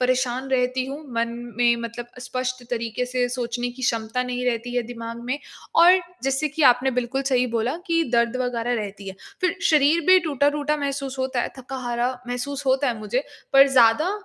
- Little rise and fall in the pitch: Yes, narrow, 2.1 semitones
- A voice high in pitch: Yes, very high, 250 Hz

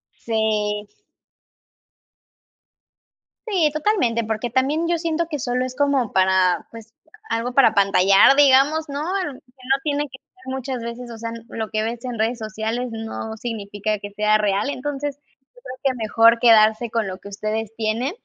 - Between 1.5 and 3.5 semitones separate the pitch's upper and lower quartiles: No, average, 4.0 semitones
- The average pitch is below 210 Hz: No, high, 235 Hz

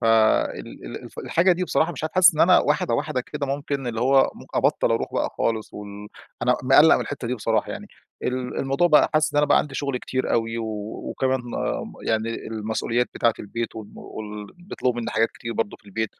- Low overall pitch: Yes, low, 125 Hz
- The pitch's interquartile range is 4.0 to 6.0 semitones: Yes, average, 4.5 semitones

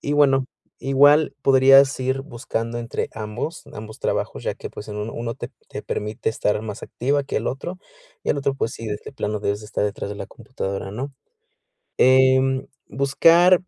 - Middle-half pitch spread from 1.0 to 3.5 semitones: No, average, 4.3 semitones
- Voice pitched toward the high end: No, low, 130 Hz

